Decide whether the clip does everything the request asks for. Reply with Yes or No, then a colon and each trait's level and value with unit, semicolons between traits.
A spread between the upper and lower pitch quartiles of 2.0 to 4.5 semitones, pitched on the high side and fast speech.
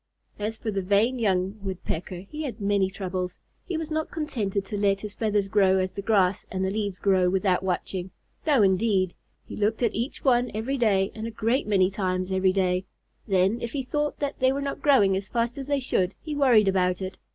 Yes: average, 3.8 semitones; high, 200 Hz; fast, 210 wpm